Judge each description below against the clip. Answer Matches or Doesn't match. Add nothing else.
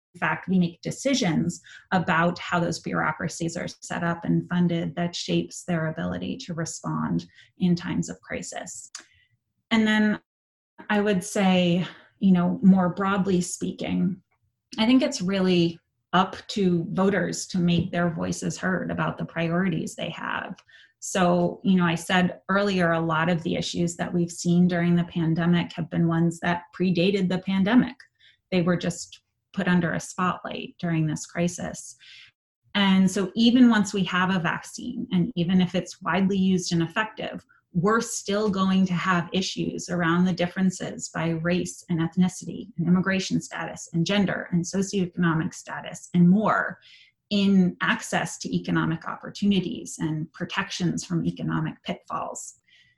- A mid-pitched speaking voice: Matches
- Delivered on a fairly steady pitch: Matches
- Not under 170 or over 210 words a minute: Doesn't match